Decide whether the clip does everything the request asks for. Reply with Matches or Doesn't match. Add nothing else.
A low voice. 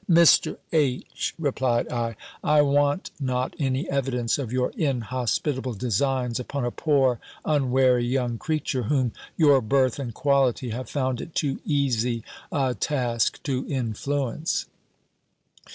Matches